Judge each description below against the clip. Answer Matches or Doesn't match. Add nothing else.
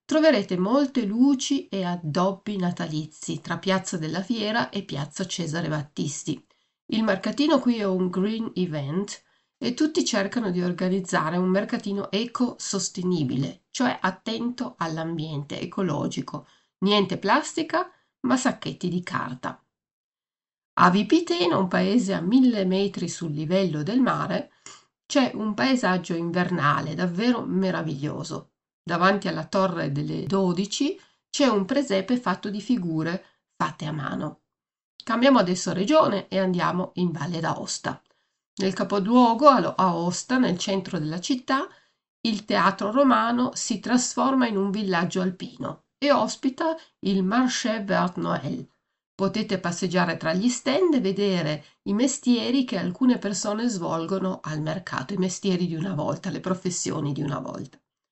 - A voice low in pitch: Doesn't match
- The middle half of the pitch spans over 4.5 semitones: Matches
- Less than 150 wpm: Matches